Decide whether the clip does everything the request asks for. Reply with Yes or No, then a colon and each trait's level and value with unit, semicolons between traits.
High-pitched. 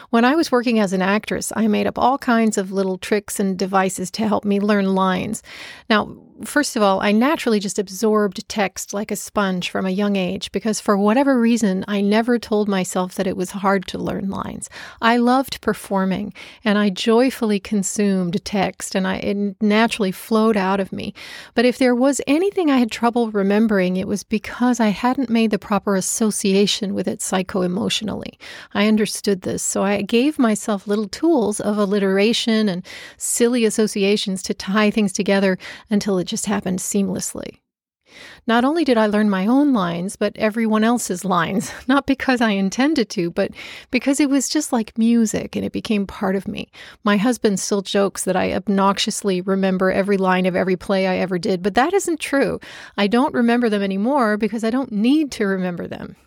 Yes: high, 210 Hz